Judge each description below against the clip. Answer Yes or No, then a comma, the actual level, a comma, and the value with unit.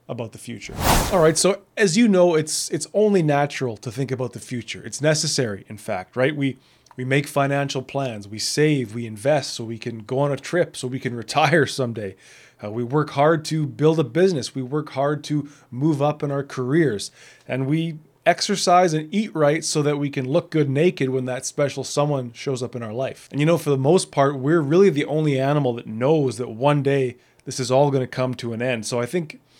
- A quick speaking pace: Yes, fast, 225 wpm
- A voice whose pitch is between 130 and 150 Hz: Yes, medium, 140 Hz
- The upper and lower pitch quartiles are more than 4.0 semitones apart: No, average, 3.3 semitones